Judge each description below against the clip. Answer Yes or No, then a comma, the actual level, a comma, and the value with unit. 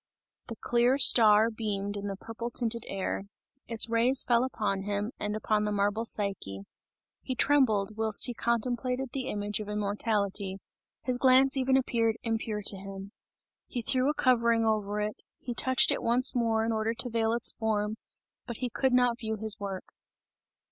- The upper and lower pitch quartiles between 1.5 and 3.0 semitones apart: Yes, average, 2.7 semitones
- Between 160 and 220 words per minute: Yes, average, 170 wpm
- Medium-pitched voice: No, high, 225 Hz